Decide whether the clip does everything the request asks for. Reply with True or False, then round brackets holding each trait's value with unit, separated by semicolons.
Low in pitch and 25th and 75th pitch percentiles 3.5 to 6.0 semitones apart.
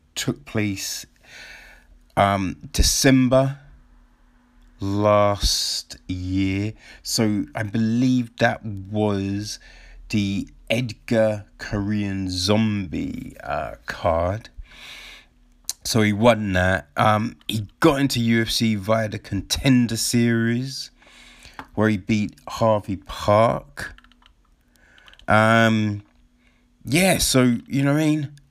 False (110 Hz; 3.0 semitones)